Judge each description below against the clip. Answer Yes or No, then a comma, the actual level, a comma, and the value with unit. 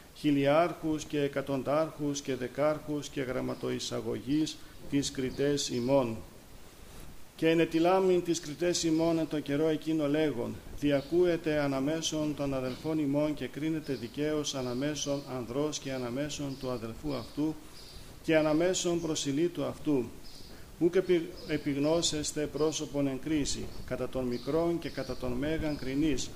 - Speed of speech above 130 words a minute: No, average, 120 wpm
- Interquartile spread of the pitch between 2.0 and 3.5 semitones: Yes, average, 2.7 semitones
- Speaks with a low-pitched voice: No, medium, 145 Hz